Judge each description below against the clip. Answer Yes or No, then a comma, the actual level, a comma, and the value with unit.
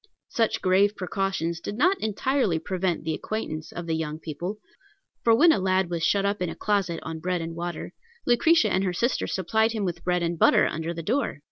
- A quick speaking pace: Yes, fast, 210 wpm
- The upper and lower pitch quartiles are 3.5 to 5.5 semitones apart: Yes, average, 4.2 semitones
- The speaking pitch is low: No, medium, 185 Hz